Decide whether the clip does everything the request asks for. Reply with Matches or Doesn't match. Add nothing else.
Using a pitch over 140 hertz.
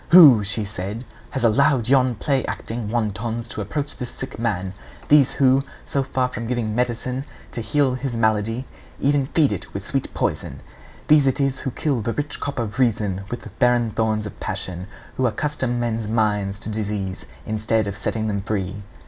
Doesn't match